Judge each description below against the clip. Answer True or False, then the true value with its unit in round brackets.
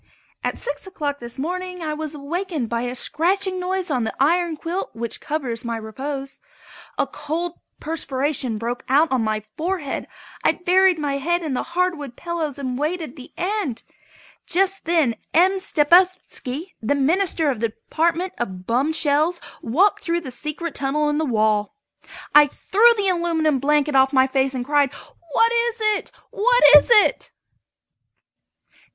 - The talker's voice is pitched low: False (300 Hz)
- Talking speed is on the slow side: False (160 wpm)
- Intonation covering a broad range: False (4.9 semitones)